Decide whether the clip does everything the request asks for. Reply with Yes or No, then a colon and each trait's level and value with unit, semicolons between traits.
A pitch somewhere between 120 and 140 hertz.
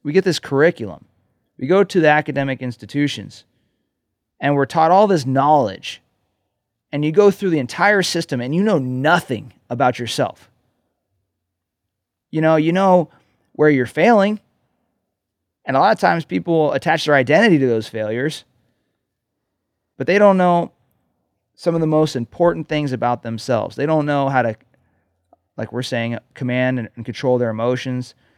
Yes: low, 135 Hz